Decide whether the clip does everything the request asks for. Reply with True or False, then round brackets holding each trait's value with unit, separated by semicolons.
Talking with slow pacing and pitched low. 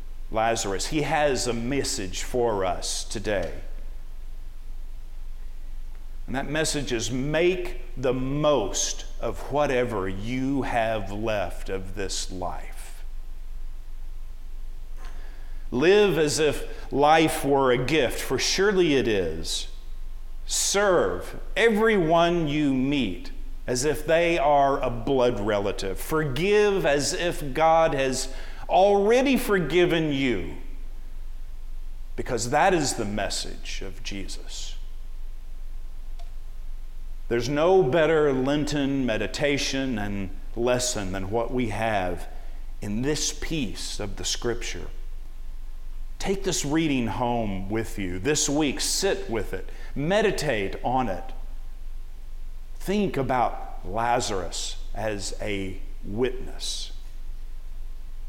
True (100 wpm; 130 Hz)